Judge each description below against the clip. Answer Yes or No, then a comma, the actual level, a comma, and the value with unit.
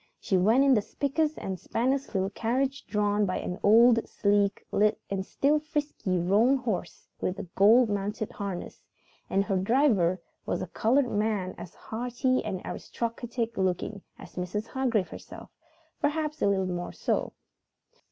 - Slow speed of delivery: No, average, 150 wpm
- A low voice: No, high, 215 Hz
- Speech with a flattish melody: No, average, 4.7 semitones